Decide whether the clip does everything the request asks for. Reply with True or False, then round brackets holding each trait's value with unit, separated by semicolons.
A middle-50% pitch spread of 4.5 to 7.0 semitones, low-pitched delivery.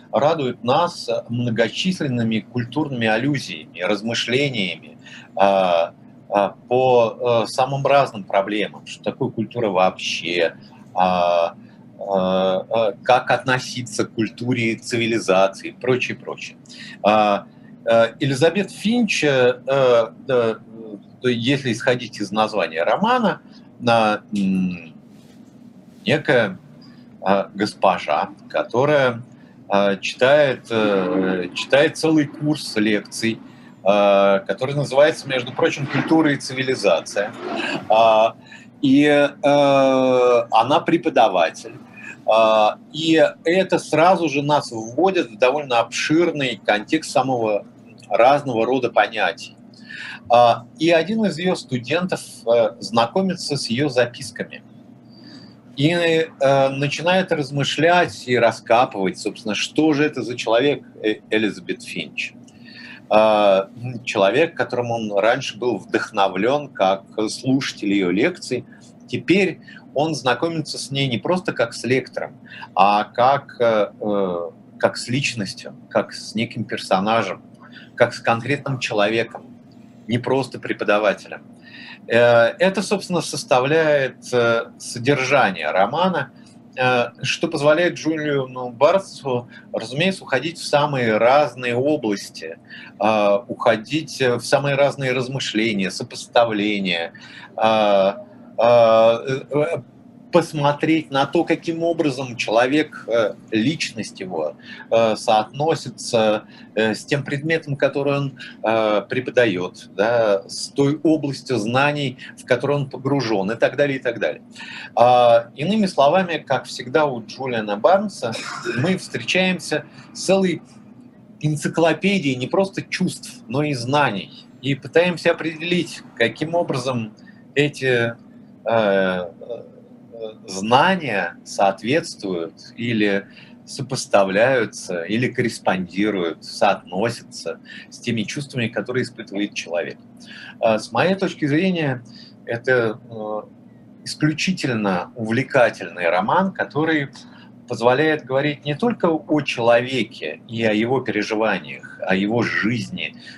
True (5.2 semitones; 125 Hz)